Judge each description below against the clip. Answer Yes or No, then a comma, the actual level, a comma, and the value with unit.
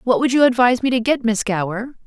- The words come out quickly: Yes, fast, 260 wpm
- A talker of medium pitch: No, high, 235 Hz